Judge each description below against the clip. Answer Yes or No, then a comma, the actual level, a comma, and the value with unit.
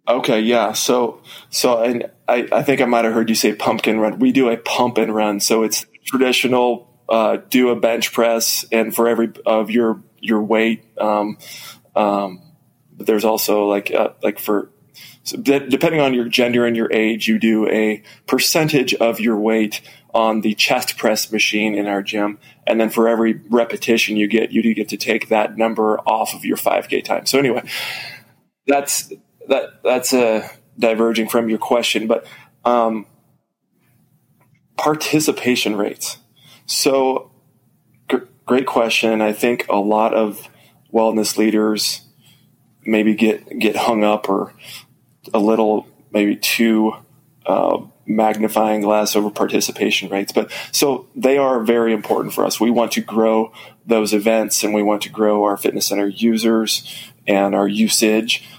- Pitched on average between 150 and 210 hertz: No, low, 110 Hz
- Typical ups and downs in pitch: No, narrow, 1.9 semitones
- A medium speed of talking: Yes, average, 160 wpm